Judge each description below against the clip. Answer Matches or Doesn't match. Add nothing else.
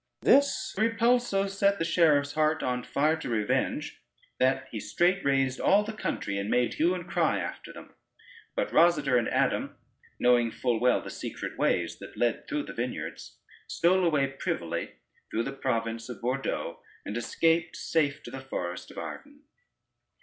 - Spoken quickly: Doesn't match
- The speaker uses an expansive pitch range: Matches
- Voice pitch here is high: Doesn't match